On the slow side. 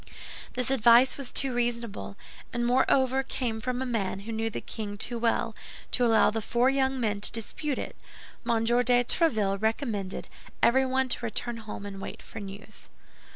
No: average, 170 wpm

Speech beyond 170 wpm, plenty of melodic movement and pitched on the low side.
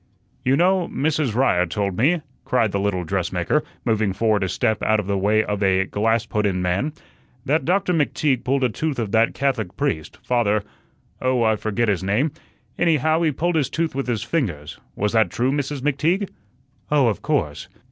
Yes: average, 190 wpm; wide, 6.2 semitones; low, 115 Hz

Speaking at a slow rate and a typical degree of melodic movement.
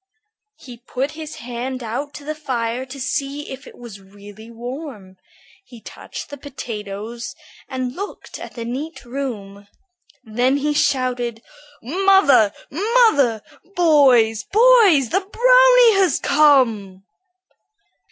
Yes: slow, 120 wpm; average, 4.8 semitones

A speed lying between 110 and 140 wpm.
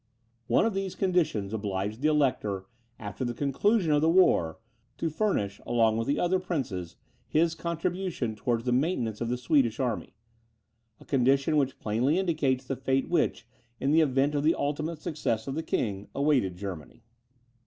No: average, 165 wpm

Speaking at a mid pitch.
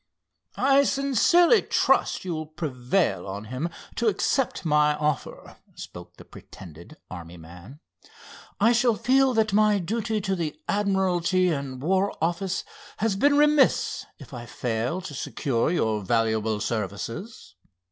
Yes: medium, 170 Hz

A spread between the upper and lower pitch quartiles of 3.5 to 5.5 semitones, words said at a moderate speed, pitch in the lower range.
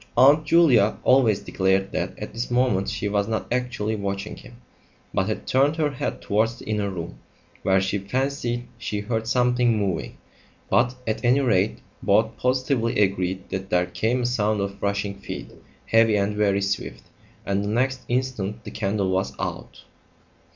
Yes: average, 3.8 semitones; average, 165 wpm; low, 110 Hz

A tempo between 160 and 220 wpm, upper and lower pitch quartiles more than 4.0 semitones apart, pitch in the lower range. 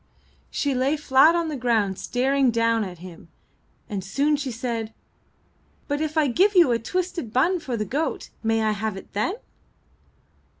No: average, 170 wpm; average, 5.3 semitones; very high, 255 Hz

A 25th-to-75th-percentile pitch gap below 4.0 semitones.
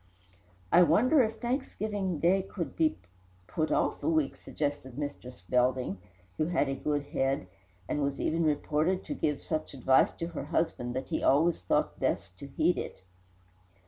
No: average, 4.4 semitones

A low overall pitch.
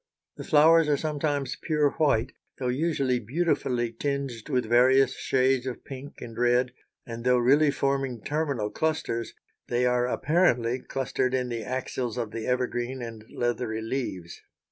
Yes: low, 125 Hz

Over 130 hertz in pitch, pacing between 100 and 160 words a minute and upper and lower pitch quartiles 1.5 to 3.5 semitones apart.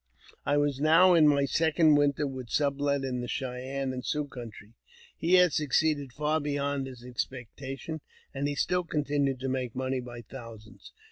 No: medium, 140 Hz; average, 175 wpm; narrow, 2.6 semitones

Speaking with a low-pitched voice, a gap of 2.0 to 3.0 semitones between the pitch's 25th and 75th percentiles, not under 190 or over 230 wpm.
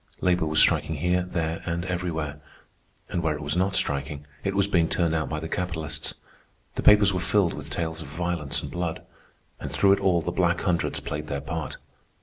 Yes: very low, 85 Hz; narrow, 2.6 semitones; average, 200 wpm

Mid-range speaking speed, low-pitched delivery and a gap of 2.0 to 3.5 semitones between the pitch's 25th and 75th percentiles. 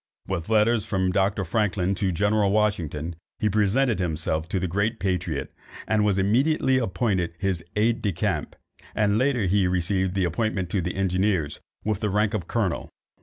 Yes: average, 170 wpm; low, 100 Hz; average, 2.9 semitones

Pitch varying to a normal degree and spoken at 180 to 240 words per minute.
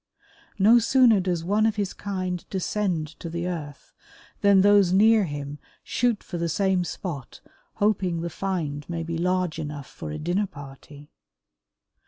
No: average, 4.2 semitones; average, 155 wpm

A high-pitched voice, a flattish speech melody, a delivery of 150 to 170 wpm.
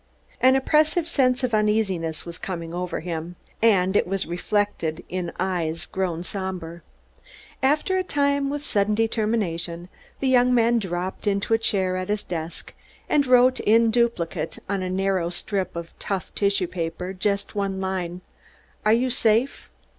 No: high, 195 Hz; average, 4.6 semitones; average, 155 wpm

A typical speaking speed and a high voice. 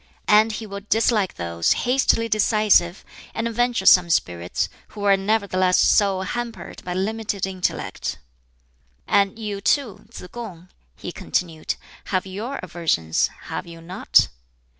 No: slow, 125 wpm; high, 200 Hz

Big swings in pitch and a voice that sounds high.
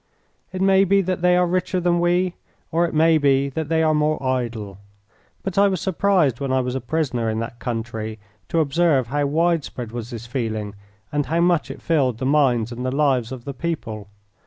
No: wide, 6.0 semitones; medium, 145 Hz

